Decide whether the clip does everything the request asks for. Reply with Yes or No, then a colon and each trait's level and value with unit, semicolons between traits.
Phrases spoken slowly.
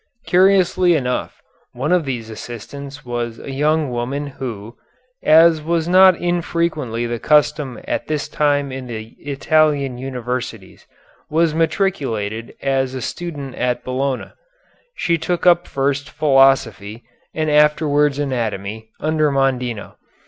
Yes: slow, 120 wpm